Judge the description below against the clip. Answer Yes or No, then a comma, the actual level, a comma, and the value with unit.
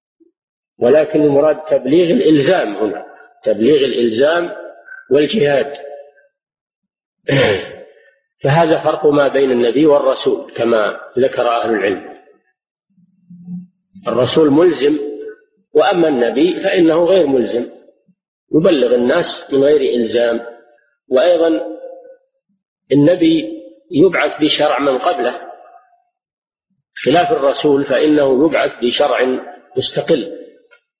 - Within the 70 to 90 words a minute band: Yes, average, 80 wpm